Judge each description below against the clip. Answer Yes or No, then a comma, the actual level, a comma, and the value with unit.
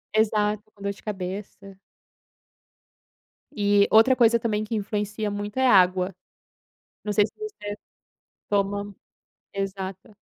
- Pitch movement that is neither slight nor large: No, narrow, 1.5 semitones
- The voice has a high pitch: Yes, high, 205 Hz